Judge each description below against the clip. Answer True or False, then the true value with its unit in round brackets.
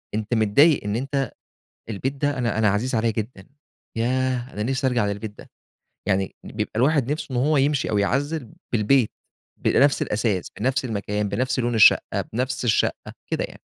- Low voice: True (120 Hz)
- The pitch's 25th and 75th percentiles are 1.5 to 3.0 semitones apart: False (4.0 semitones)